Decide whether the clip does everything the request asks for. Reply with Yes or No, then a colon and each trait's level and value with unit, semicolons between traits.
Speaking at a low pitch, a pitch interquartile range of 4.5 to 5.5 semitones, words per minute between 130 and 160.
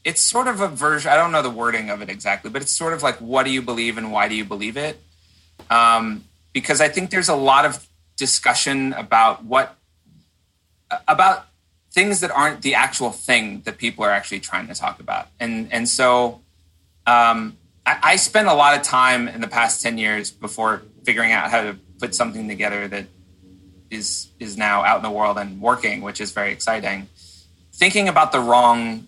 No: low, 115 Hz; average, 5.1 semitones; average, 200 wpm